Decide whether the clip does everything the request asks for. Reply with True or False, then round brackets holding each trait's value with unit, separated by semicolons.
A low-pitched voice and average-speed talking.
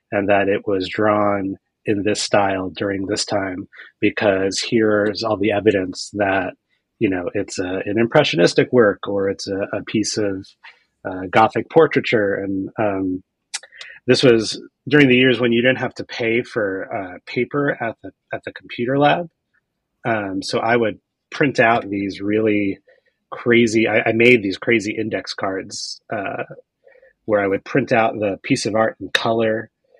True (110 Hz; 170 wpm)